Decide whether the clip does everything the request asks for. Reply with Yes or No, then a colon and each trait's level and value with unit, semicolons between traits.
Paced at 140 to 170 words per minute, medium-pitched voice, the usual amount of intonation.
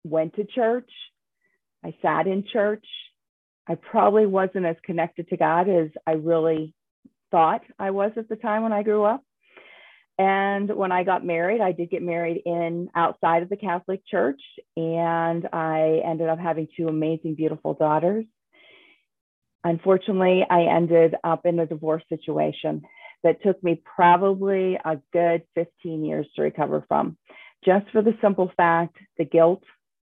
Yes: average, 155 wpm; medium, 175 Hz; average, 3.0 semitones